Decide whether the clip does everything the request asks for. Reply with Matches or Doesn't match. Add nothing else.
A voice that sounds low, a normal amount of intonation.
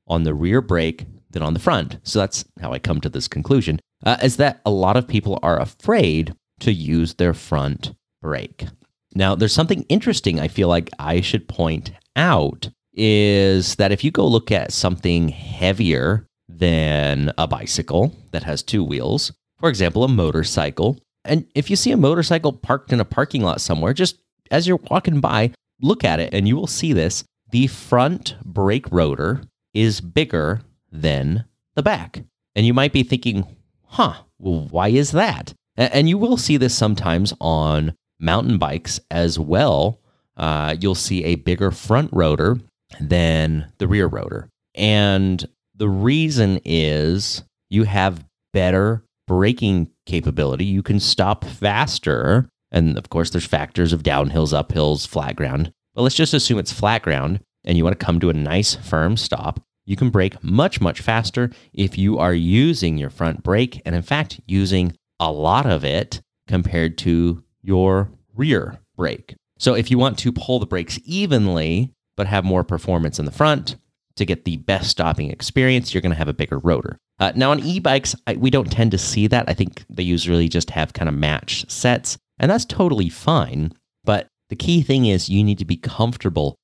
Doesn't match